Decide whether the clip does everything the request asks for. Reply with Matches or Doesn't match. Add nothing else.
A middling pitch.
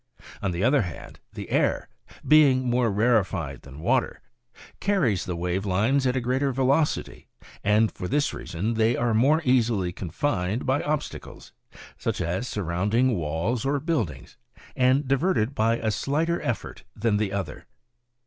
Doesn't match